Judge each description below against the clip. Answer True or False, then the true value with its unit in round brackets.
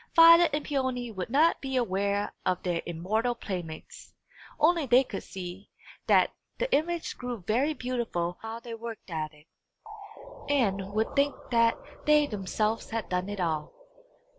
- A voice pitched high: True (225 Hz)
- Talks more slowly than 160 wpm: True (150 wpm)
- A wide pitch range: True (6.1 semitones)